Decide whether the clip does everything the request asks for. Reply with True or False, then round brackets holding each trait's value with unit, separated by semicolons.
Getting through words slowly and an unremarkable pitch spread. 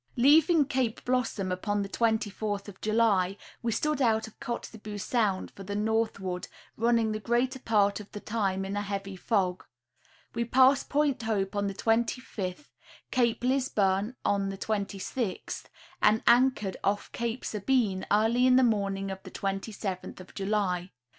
False (155 wpm; 3.3 semitones)